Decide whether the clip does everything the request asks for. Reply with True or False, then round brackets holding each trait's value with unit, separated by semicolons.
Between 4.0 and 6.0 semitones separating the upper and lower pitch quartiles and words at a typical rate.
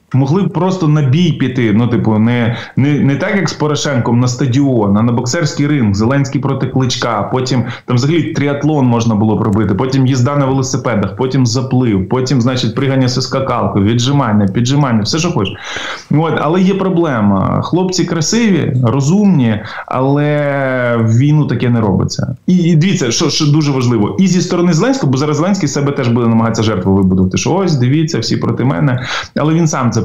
False (4.4 semitones; 175 wpm)